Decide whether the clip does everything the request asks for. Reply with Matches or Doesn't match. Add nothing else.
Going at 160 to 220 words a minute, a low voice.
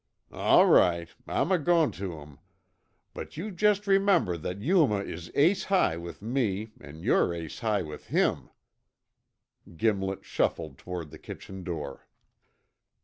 Doesn't match